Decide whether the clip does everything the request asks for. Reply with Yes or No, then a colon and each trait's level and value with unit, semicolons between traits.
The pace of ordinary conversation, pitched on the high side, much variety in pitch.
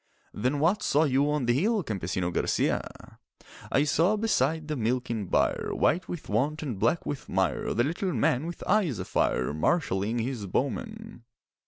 No: average, 160 wpm; medium, 140 Hz; wide, 6.9 semitones